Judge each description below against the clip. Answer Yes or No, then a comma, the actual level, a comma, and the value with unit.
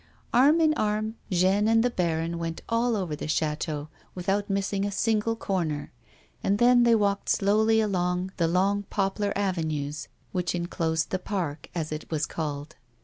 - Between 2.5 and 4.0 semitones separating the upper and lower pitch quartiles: No, average, 4.4 semitones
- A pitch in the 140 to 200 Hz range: Yes, high, 190 Hz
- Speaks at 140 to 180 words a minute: Yes, average, 160 wpm